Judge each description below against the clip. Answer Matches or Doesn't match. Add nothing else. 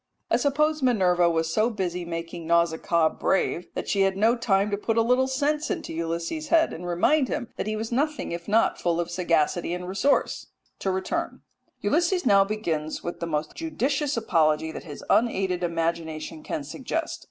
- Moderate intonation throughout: Doesn't match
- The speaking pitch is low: Doesn't match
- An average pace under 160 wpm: Doesn't match